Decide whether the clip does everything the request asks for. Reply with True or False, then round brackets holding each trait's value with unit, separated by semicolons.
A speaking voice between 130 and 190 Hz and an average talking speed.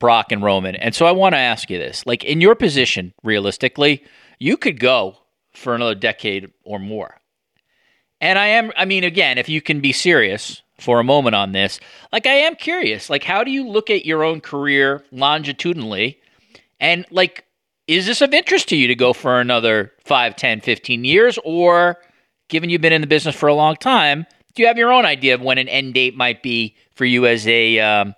False (140 Hz; 210 wpm)